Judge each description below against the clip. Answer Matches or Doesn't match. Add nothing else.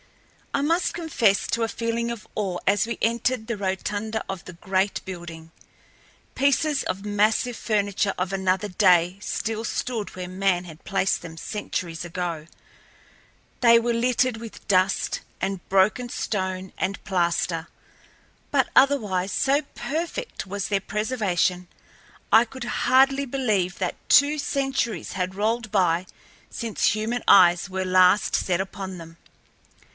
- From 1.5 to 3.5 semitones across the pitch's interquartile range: Doesn't match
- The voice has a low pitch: Doesn't match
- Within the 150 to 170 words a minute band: Doesn't match